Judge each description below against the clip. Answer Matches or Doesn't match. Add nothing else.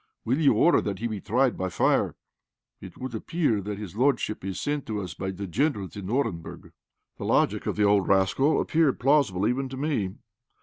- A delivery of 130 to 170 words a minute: Doesn't match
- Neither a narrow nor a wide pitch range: Doesn't match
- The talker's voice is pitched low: Matches